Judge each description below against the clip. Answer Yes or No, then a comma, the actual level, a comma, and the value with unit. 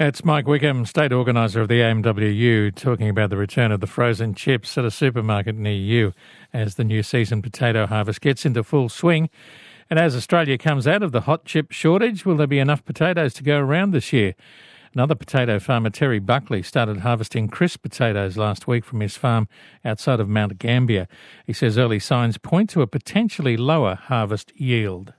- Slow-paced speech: No, average, 190 wpm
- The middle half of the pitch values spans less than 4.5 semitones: No, average, 5.2 semitones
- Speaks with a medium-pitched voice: No, low, 120 Hz